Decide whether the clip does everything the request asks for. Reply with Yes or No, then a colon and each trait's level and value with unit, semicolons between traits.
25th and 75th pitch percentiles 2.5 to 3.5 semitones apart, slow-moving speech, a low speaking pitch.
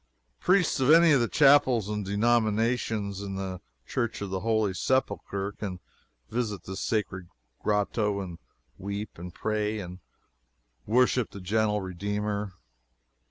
Yes: average, 2.9 semitones; slow, 130 wpm; low, 105 Hz